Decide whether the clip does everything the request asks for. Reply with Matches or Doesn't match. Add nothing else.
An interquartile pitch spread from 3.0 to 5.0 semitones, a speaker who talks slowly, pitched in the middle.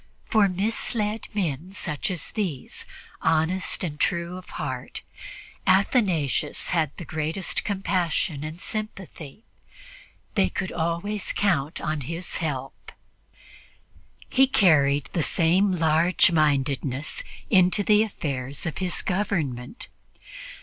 Matches